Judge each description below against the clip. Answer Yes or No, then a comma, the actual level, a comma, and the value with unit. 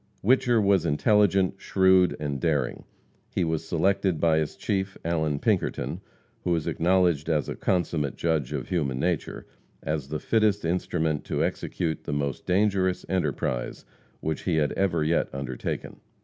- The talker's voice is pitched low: Yes, very low, 85 Hz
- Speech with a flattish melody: No, average, 3.9 semitones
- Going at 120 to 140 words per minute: No, average, 150 wpm